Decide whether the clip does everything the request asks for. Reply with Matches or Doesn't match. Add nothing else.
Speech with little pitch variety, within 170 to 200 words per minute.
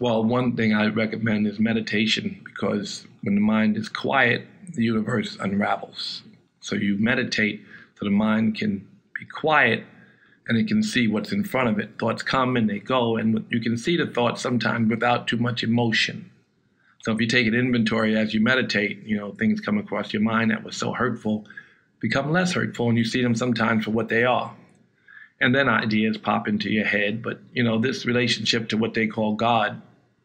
Matches